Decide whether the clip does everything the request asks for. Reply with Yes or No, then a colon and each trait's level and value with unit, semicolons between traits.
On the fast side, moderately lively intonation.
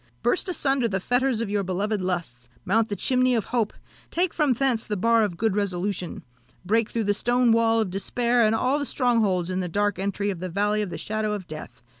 Yes: fast, 220 wpm; average, 4.0 semitones